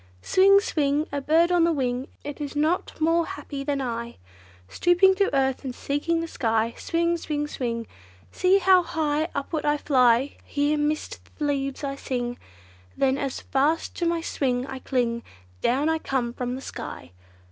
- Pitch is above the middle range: Yes, very high, 290 Hz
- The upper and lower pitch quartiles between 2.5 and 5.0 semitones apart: Yes, average, 4.0 semitones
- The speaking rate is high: No, average, 170 wpm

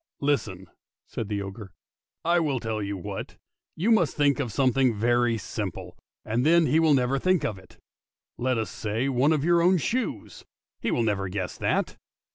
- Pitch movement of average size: No, wide, 6.1 semitones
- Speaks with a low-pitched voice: Yes, low, 125 Hz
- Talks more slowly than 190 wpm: No, average, 195 wpm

